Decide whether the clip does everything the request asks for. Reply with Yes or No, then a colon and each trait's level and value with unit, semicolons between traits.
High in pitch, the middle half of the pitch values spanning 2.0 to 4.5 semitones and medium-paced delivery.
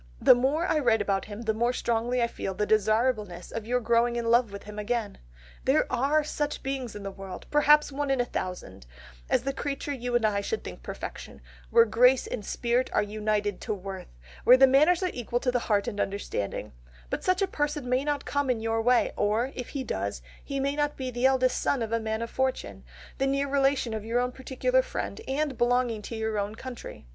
No: high, 245 Hz; average, 3.9 semitones; fast, 220 wpm